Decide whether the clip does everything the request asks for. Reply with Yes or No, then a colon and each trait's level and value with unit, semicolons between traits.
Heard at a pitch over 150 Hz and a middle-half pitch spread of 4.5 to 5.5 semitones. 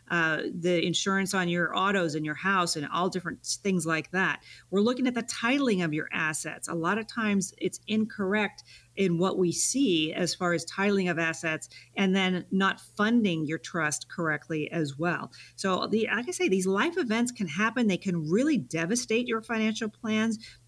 Yes: medium, 185 Hz; average, 4.8 semitones